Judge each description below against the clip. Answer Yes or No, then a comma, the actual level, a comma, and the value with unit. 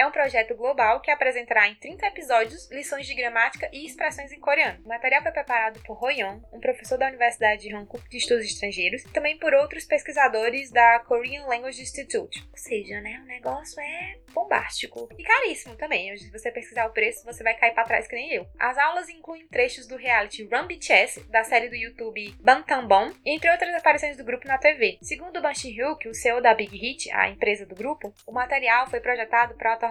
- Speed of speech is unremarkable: No, fast, 205 wpm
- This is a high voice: Yes, very high, 255 Hz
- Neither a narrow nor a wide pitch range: Yes, average, 4.4 semitones